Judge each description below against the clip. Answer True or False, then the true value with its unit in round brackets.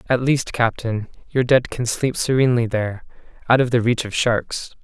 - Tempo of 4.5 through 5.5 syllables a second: True (5.0 syllables/s)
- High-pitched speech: False (120 Hz)